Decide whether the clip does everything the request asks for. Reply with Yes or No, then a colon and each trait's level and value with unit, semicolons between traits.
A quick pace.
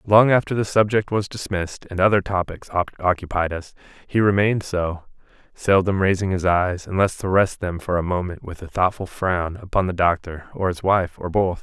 No: average, 190 wpm